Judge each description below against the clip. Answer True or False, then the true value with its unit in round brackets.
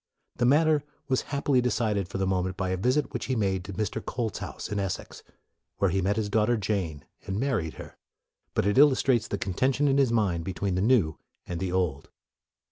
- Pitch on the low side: True (105 Hz)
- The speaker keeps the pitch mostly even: False (5.1 semitones)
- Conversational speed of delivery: False (210 wpm)